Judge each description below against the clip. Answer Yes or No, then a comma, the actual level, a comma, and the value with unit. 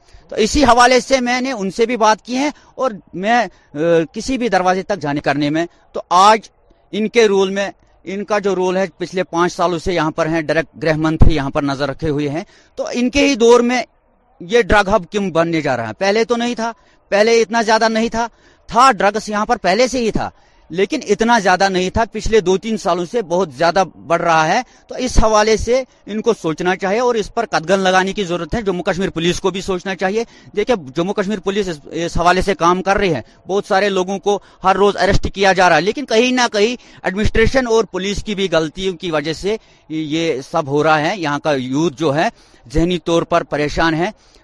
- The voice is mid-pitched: No, high, 195 Hz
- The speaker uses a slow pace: No, fast, 225 wpm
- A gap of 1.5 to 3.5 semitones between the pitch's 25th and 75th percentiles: No, average, 5.0 semitones